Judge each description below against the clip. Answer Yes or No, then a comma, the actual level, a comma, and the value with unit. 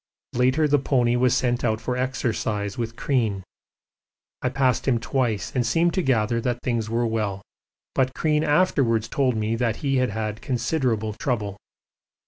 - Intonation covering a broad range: No, average, 2.9 semitones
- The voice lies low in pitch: Yes, low, 120 Hz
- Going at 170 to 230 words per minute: No, average, 160 wpm